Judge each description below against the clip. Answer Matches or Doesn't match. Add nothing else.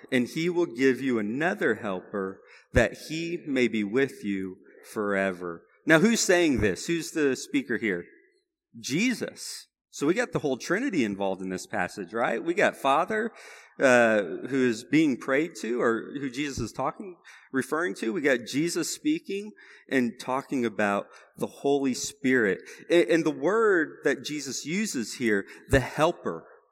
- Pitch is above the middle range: Doesn't match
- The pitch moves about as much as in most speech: Doesn't match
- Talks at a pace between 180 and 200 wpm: Doesn't match